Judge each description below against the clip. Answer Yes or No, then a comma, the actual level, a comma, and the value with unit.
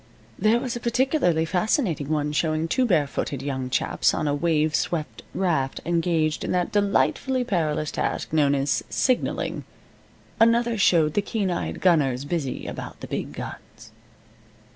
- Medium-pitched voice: Yes, medium, 165 Hz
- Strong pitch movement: Yes, wide, 5.7 semitones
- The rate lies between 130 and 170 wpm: Yes, average, 145 wpm